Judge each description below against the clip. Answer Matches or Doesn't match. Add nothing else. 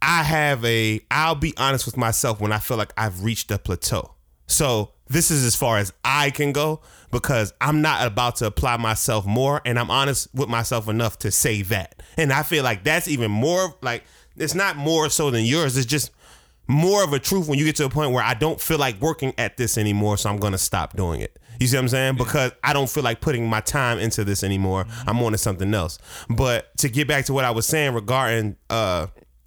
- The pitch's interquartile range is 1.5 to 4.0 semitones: Doesn't match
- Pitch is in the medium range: Doesn't match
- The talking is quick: Matches